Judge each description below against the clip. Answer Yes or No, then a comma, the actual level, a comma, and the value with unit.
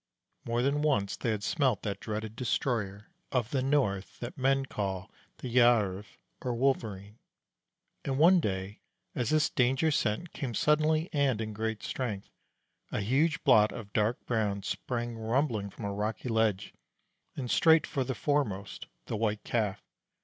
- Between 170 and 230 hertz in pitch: No, low, 115 Hz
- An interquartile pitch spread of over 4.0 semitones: Yes, average, 4.4 semitones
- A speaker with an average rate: Yes, average, 155 wpm